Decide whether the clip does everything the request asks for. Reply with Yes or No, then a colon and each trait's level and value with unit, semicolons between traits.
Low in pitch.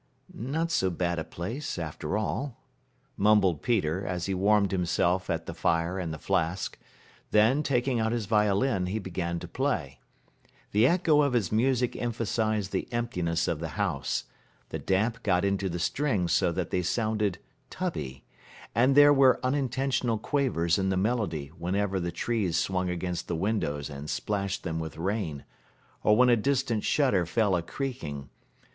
Yes: low, 100 Hz